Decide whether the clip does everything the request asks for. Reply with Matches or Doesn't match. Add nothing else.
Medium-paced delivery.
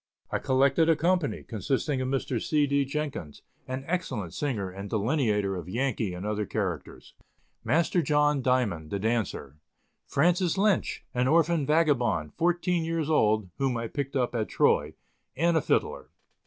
Matches